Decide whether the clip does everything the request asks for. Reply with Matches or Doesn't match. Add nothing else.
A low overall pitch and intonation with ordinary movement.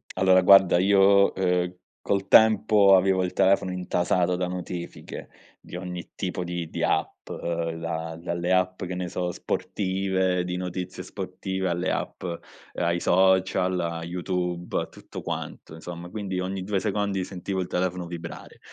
Doesn't match